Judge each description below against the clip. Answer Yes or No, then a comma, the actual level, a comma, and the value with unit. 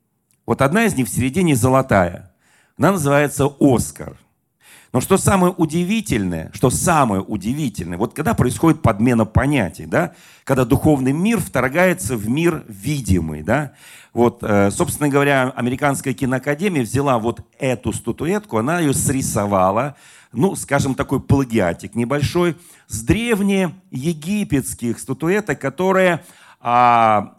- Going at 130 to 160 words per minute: No, average, 115 wpm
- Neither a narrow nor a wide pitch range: No, wide, 5.8 semitones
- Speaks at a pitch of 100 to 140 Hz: Yes, low, 135 Hz